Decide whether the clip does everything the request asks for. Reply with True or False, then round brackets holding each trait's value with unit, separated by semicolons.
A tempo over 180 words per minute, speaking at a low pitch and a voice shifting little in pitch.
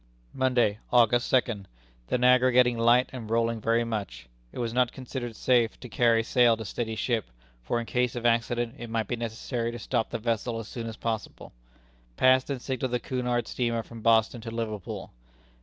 True (190 wpm; 115 Hz; 1.5 semitones)